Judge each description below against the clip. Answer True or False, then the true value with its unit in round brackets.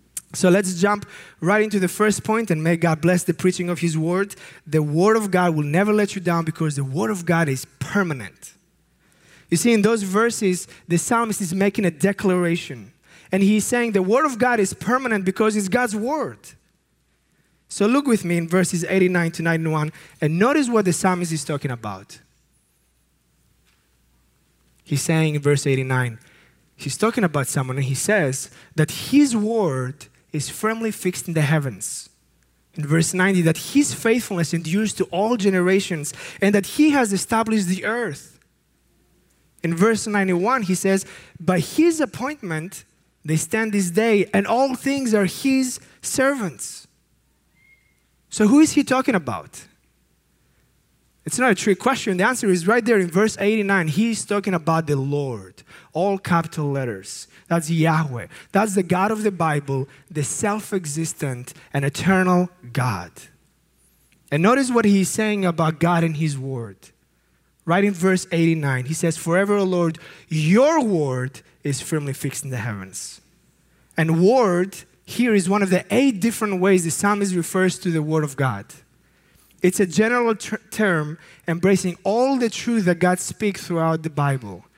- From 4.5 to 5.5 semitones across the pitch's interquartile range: True (5.2 semitones)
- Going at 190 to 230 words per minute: False (165 wpm)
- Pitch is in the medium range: True (180 Hz)